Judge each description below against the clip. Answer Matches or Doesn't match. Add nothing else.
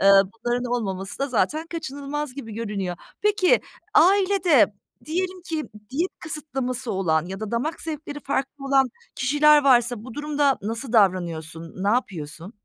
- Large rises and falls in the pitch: Matches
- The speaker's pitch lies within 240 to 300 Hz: Matches